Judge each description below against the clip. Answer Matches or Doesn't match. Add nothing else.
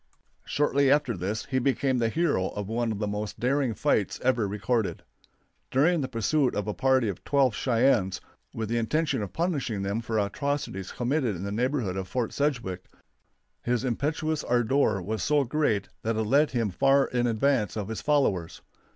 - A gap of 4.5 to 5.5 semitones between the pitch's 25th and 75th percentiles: Matches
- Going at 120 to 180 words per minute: Matches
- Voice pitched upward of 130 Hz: Doesn't match